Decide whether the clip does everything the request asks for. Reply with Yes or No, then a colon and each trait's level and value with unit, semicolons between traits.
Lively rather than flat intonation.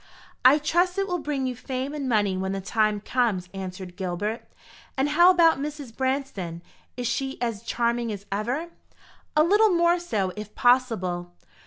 Yes: wide, 6.7 semitones